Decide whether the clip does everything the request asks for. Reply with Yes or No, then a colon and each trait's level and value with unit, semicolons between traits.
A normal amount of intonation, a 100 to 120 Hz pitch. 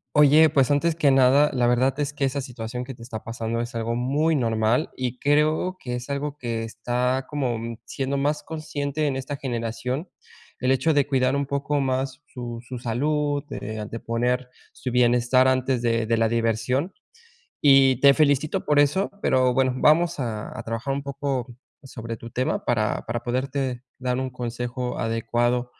No: average, 3.0 semitones; low, 130 Hz